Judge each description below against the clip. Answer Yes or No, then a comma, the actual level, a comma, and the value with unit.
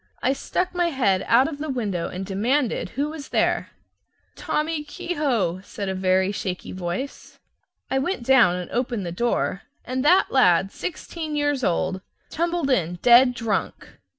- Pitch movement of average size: No, wide, 7.5 semitones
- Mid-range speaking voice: No, high, 245 Hz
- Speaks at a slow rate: No, average, 155 wpm